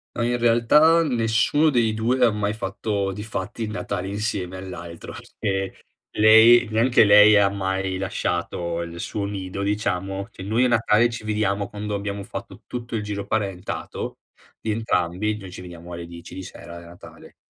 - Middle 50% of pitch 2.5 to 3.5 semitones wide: Yes, average, 2.9 semitones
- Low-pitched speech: Yes, low, 105 Hz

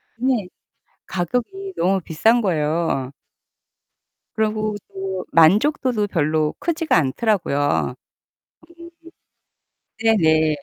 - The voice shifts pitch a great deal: Yes, wide, 6.1 semitones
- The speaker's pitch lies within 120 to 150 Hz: No, high, 190 Hz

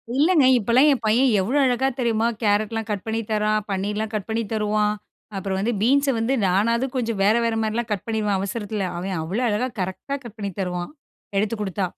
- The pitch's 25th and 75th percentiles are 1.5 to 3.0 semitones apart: Yes, average, 2.7 semitones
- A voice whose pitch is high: Yes, high, 215 Hz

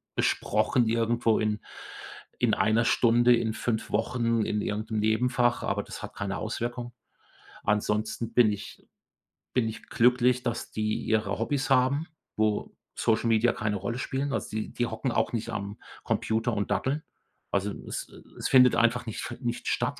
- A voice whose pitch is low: Yes, low, 115 Hz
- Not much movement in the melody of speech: Yes, narrow, 2.1 semitones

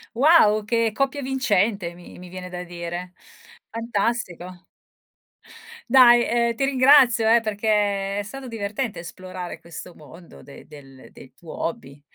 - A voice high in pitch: Yes, high, 205 Hz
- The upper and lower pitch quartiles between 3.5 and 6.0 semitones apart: Yes, average, 5.0 semitones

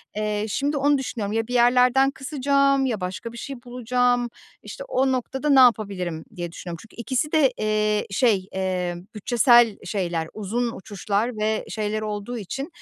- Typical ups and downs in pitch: Yes, average, 4.0 semitones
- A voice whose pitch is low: No, high, 230 Hz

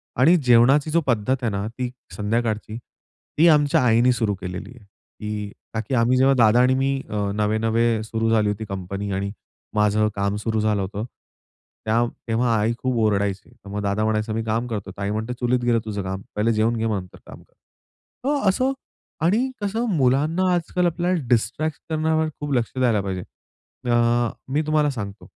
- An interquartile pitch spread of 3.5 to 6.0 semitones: Yes, average, 4.0 semitones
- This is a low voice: Yes, low, 115 Hz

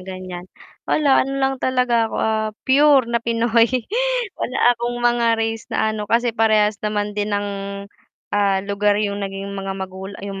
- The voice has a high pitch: Yes, high, 215 Hz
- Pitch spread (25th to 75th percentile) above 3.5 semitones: No, average, 2.9 semitones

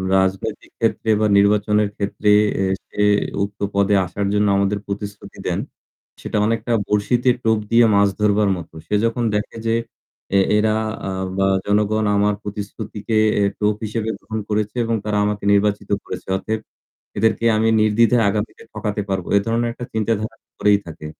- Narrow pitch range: Yes, narrow, 1.5 semitones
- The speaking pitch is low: Yes, low, 105 Hz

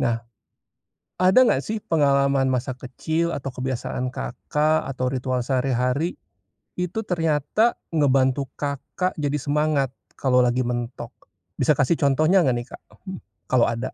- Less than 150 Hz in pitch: Yes, low, 135 Hz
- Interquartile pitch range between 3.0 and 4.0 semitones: Yes, average, 3.5 semitones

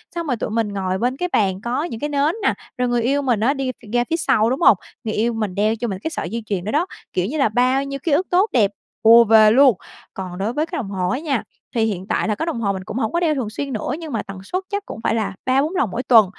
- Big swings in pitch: No, average, 4.9 semitones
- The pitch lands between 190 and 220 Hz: No, high, 235 Hz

